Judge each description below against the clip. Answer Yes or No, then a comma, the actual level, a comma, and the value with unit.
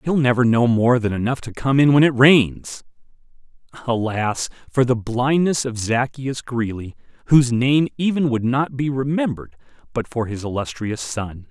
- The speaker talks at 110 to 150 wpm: No, average, 160 wpm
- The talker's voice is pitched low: Yes, low, 125 Hz